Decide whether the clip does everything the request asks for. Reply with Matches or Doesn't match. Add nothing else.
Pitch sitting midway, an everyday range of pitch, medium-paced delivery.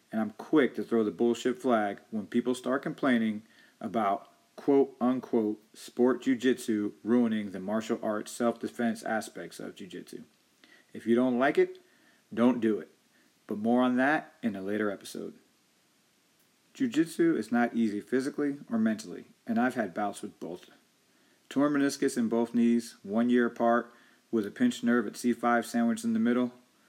Doesn't match